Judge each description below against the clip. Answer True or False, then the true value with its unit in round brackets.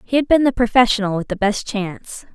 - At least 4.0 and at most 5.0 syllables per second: False (5.9 syllables/s)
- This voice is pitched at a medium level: False (225 Hz)